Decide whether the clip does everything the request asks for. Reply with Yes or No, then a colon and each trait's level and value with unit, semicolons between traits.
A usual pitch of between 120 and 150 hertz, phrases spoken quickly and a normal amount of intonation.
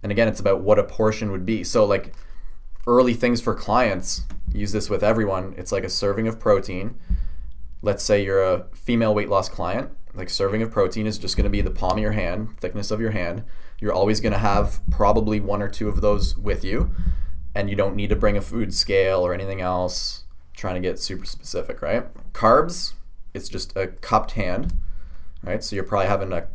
No: low, 100 Hz; fast, 215 wpm; average, 3.5 semitones